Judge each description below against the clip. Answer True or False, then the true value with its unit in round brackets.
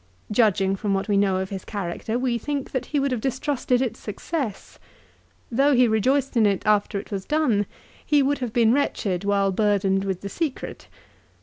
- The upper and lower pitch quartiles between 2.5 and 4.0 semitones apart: False (4.8 semitones)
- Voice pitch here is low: False (220 Hz)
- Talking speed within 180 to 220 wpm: True (190 wpm)